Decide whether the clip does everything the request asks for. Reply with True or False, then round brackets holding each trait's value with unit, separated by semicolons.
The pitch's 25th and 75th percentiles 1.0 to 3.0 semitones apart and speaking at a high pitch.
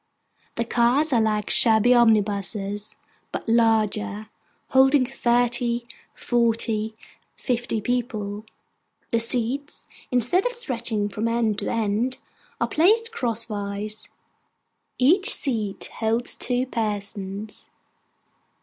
True (2.6 semitones; 230 Hz)